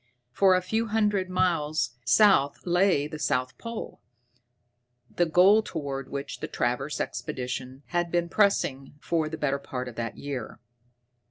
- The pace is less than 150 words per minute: Yes, average, 140 wpm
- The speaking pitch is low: No, medium, 155 Hz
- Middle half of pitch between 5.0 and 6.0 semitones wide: Yes, wide, 5.4 semitones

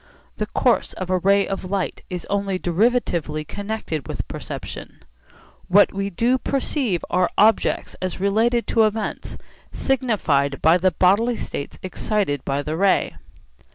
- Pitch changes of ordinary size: Yes, average, 3.9 semitones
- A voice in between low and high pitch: No, high, 195 Hz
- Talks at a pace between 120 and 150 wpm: Yes, average, 140 wpm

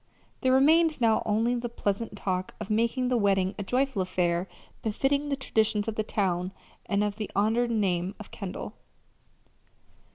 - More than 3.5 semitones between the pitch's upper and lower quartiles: Yes, average, 3.9 semitones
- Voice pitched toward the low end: No, high, 215 Hz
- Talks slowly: No, average, 160 wpm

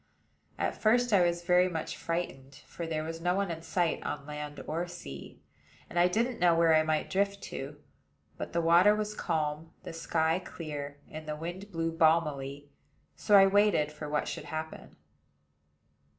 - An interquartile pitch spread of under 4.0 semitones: Yes, average, 2.9 semitones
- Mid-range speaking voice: Yes, medium, 165 Hz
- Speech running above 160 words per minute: Yes, average, 175 wpm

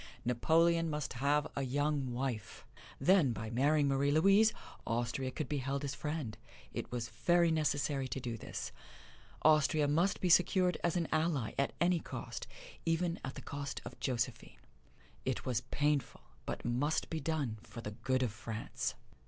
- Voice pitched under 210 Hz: Yes, medium, 140 Hz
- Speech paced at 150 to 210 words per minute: Yes, average, 160 wpm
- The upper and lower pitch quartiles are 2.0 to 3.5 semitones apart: No, average, 4.3 semitones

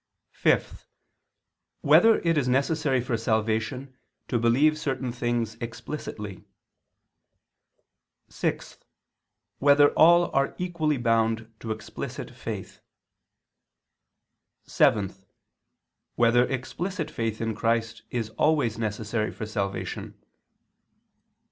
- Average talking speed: No, slow, 90 wpm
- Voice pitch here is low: Yes, low, 120 Hz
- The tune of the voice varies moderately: Yes, average, 4.3 semitones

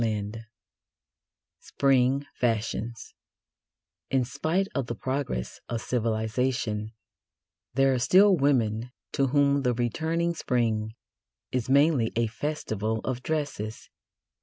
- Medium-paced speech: No, slow, 105 wpm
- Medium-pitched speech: No, low, 125 Hz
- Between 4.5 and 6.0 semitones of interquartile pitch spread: No, average, 4.0 semitones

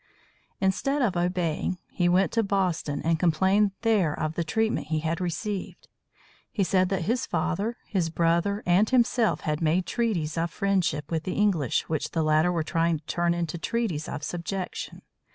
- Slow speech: No, average, 170 wpm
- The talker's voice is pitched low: No, medium, 175 Hz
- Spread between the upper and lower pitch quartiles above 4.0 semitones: No, average, 3.6 semitones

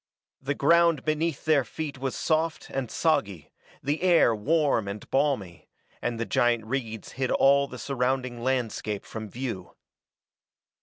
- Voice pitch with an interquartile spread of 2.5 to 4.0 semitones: No, average, 4.6 semitones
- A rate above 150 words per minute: No, average, 140 wpm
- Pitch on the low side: Yes, low, 130 Hz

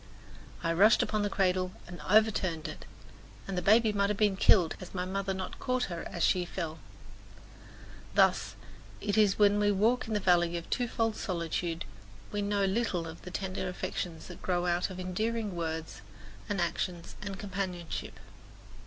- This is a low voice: No, high, 190 Hz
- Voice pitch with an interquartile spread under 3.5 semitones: Yes, average, 2.9 semitones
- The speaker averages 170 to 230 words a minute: Yes, average, 175 wpm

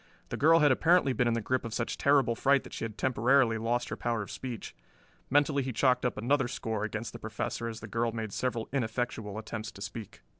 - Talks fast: Yes, fast, 225 wpm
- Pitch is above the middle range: No, low, 120 Hz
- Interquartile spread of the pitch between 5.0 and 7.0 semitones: No, average, 2.9 semitones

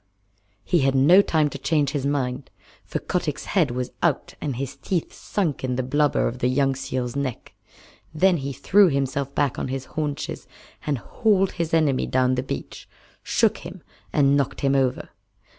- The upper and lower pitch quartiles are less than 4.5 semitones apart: Yes, average, 3.1 semitones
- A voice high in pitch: No, medium, 140 Hz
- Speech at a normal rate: Yes, average, 175 wpm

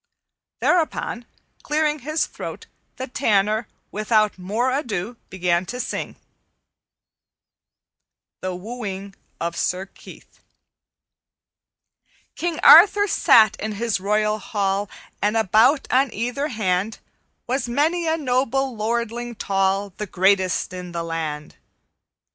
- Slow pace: Yes, slow, 105 wpm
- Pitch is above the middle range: Yes, high, 215 Hz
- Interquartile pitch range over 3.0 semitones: Yes, average, 4.9 semitones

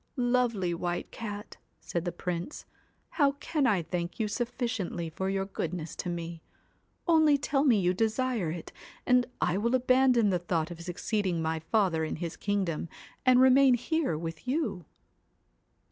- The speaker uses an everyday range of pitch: No, wide, 6.5 semitones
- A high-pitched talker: Yes, high, 200 Hz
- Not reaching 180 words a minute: Yes, average, 155 wpm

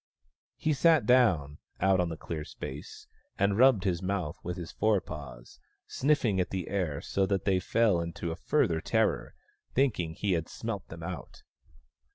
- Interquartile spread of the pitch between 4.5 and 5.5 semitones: No, average, 4.1 semitones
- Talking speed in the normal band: Yes, average, 165 wpm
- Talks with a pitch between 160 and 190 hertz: No, very low, 95 Hz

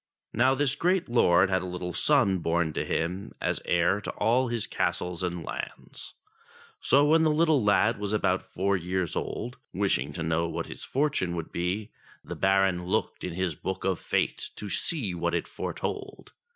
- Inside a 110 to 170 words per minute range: No, average, 180 wpm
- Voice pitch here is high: No, very low, 95 Hz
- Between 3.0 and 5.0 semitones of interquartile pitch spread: No, wide, 5.4 semitones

